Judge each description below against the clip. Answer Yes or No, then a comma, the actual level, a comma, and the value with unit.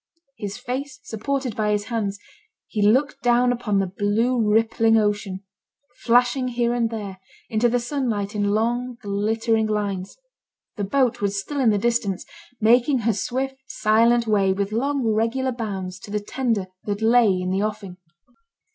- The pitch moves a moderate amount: Yes, average, 3.0 semitones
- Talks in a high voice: Yes, high, 220 Hz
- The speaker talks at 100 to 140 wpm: No, average, 155 wpm